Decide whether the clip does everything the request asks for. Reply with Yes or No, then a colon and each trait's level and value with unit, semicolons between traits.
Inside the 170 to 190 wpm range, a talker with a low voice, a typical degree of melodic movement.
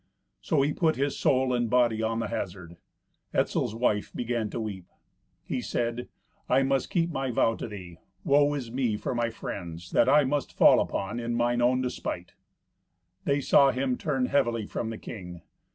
Yes: average, 180 wpm; low, 120 Hz; average, 3.5 semitones